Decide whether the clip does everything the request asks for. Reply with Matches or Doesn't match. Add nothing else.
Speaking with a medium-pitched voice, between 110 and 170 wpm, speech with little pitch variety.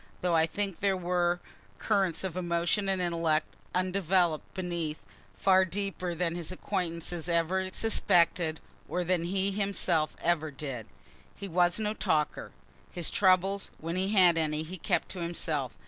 Matches